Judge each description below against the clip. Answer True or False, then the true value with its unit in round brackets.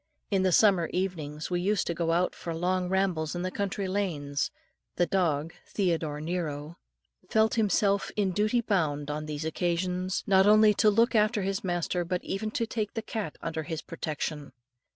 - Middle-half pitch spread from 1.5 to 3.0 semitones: False (3.9 semitones)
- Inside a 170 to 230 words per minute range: True (175 wpm)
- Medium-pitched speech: True (180 Hz)